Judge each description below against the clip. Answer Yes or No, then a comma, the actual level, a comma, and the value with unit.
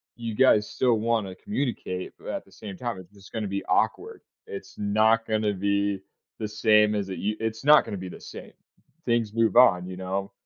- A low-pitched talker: Yes, low, 105 Hz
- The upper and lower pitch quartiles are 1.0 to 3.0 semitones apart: Yes, average, 2.7 semitones